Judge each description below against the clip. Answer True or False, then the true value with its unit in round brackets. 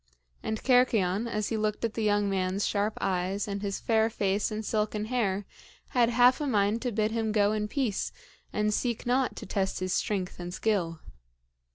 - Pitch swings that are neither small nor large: False (2.3 semitones)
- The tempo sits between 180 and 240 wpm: True (190 wpm)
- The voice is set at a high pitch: True (210 Hz)